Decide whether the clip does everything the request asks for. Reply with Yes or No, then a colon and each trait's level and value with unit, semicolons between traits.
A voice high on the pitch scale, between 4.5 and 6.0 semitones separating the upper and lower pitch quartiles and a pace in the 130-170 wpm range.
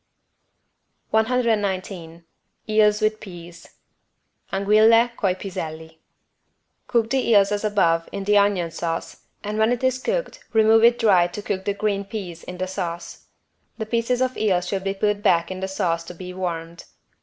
No: high, 200 Hz; average, 3.7 semitones; average, 160 wpm